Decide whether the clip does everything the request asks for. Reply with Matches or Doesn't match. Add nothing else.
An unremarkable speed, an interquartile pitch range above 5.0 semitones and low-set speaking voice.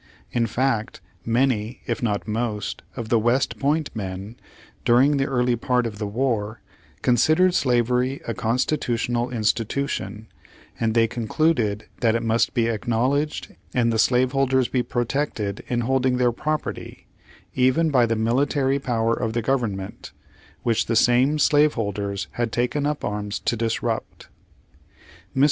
Doesn't match